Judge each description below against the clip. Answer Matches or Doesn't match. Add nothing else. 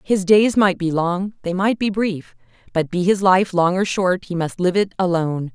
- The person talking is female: Matches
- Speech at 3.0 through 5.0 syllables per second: Matches